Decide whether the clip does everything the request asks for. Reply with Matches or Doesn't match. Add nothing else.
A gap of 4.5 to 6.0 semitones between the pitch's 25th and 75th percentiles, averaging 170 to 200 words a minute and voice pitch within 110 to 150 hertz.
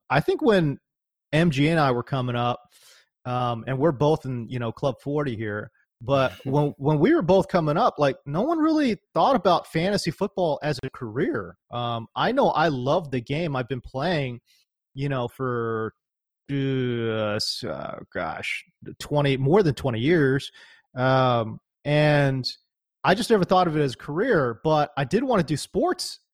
Matches